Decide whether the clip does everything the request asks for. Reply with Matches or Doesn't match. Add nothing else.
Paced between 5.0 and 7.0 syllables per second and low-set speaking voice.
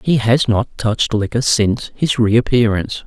Doesn't match